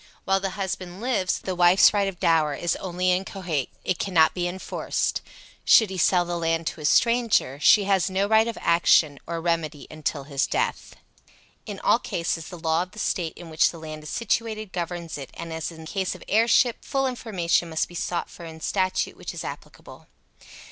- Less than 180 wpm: No, average, 200 wpm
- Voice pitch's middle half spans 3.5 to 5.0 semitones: No, average, 3.0 semitones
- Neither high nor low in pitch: Yes, medium, 175 Hz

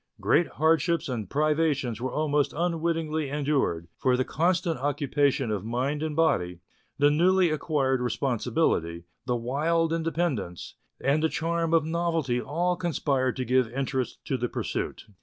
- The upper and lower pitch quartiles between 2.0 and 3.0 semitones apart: No, average, 4.3 semitones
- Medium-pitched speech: Yes, medium, 145 Hz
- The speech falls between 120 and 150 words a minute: Yes, average, 145 wpm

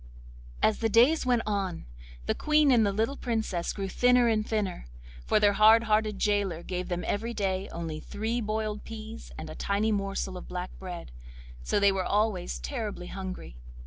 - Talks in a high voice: Yes, high, 210 Hz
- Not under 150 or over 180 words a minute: Yes, average, 175 wpm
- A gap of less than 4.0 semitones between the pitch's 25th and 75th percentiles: Yes, average, 3.1 semitones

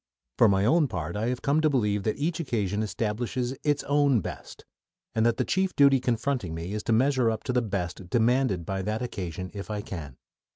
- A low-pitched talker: Yes, low, 115 Hz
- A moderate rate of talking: No, fast, 210 wpm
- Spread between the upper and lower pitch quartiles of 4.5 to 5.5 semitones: Yes, average, 5.0 semitones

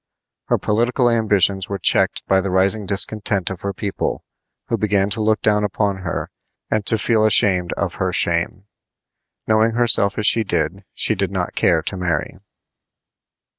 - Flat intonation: Yes, narrow, 2.3 semitones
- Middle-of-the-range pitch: No, low, 100 Hz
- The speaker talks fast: No, average, 165 wpm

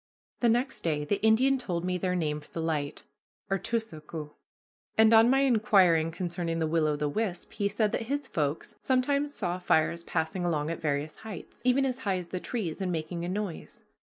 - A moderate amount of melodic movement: No, wide, 5.7 semitones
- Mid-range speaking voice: Yes, medium, 180 Hz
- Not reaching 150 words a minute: No, average, 195 wpm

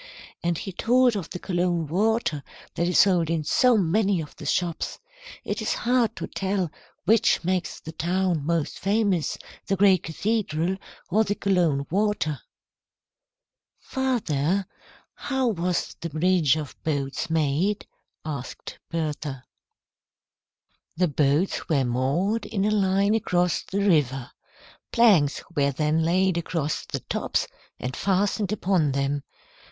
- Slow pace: Yes, slow, 130 wpm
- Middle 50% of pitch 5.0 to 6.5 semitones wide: No, average, 4.6 semitones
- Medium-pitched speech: Yes, medium, 175 Hz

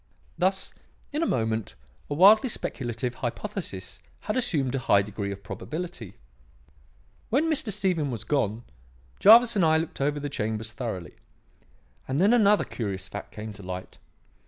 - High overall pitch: No, low, 135 Hz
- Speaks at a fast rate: No, average, 150 wpm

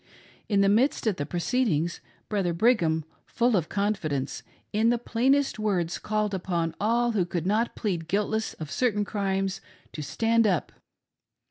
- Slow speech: No, average, 155 wpm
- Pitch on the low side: No, high, 205 Hz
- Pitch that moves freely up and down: No, average, 4.6 semitones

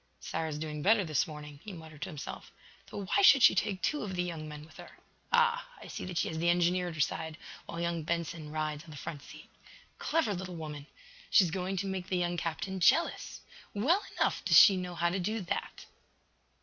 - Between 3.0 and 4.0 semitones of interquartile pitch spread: Yes, average, 3.4 semitones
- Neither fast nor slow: No, fast, 225 wpm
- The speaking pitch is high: No, medium, 175 Hz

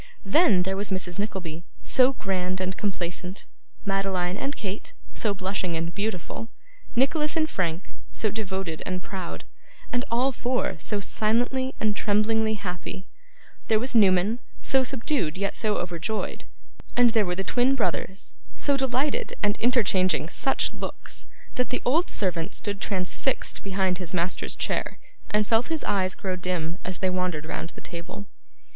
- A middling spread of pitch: Yes, average, 4.2 semitones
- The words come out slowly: No, average, 150 wpm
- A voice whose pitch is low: No, high, 200 Hz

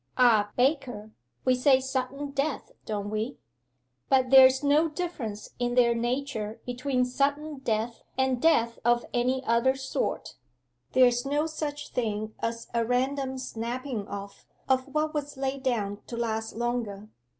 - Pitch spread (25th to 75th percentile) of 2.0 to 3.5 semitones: Yes, average, 3.0 semitones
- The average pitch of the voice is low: No, very high, 255 Hz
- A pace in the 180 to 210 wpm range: No, average, 140 wpm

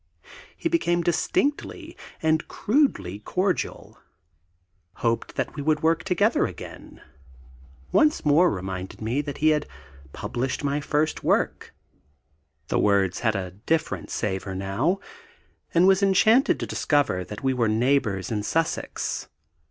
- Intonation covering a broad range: Yes, wide, 8.6 semitones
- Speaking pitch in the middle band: Yes, medium, 145 Hz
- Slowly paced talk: Yes, slow, 130 wpm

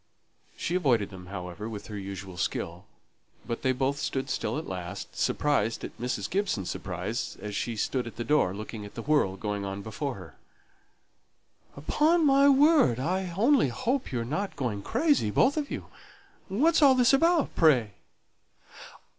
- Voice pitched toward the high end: No, low, 125 Hz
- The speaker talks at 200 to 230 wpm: No, average, 165 wpm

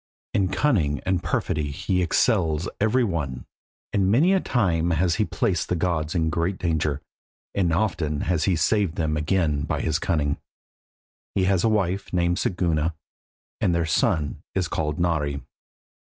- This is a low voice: Yes, very low, 85 Hz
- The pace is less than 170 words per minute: Yes, average, 155 wpm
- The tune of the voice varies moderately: Yes, average, 3.7 semitones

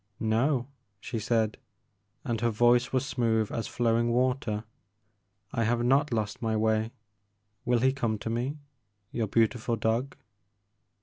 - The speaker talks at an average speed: Yes, average, 145 wpm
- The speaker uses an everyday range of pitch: No, narrow, 1.9 semitones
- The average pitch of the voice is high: No, low, 115 Hz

